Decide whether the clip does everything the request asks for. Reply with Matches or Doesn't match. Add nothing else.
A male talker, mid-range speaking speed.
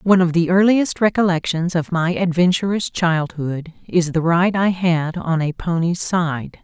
Doesn't match